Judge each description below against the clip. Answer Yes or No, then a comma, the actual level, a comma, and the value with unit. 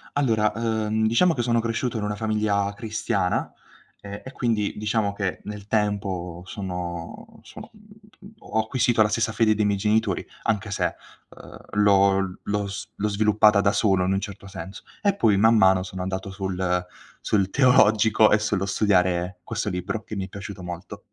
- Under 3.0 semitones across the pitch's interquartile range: Yes, narrow, 2.4 semitones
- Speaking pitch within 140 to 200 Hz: No, low, 105 Hz